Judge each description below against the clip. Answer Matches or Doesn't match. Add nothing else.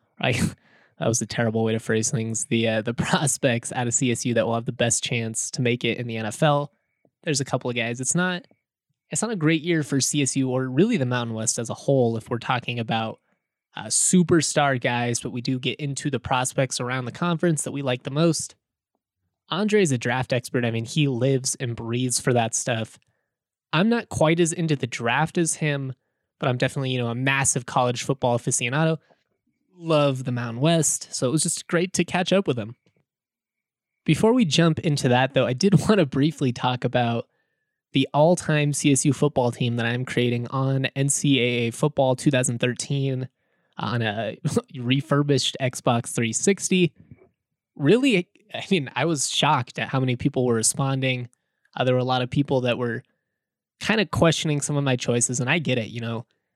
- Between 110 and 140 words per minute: Doesn't match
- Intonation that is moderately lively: Matches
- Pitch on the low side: Matches